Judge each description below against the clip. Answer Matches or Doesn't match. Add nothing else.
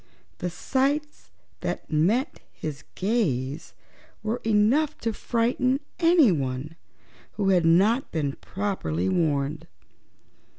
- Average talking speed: Doesn't match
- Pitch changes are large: Matches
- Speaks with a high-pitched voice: Matches